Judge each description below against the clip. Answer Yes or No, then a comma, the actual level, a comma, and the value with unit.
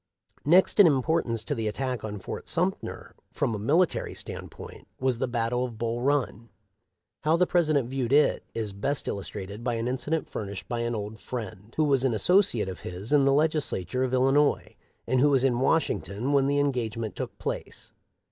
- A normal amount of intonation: Yes, average, 4.2 semitones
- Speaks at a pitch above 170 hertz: No, low, 125 Hz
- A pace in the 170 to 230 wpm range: Yes, average, 195 wpm